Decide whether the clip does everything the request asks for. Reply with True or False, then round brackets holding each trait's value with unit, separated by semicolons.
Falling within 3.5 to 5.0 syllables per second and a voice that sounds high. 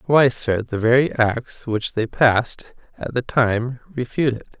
False (4.1 syllables/s; 120 Hz)